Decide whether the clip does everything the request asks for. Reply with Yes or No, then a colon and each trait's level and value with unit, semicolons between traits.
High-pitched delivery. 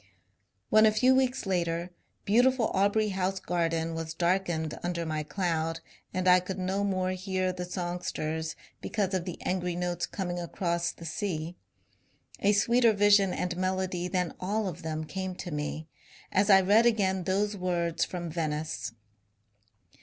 No: medium, 180 Hz